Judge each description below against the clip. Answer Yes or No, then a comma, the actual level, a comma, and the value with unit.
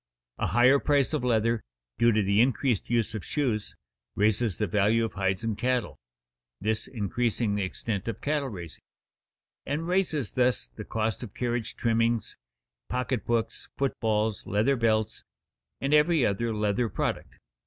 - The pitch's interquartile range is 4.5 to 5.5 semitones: No, average, 3.0 semitones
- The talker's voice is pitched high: No, low, 115 Hz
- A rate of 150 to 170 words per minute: Yes, average, 155 wpm